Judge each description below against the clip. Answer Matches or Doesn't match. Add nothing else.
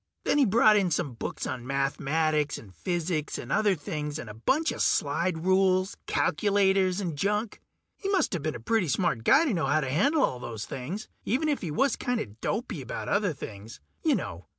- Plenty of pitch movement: Matches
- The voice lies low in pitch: Doesn't match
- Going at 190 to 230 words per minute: Matches